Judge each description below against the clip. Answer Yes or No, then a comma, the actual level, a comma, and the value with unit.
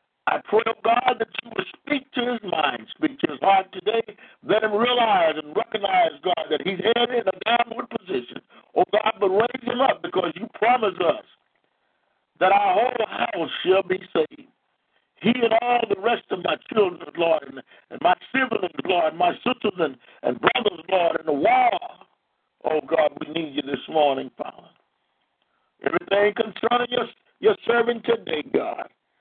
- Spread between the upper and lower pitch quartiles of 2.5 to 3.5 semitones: No, average, 4.9 semitones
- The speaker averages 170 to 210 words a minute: Yes, average, 175 wpm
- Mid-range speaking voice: No, high, 225 Hz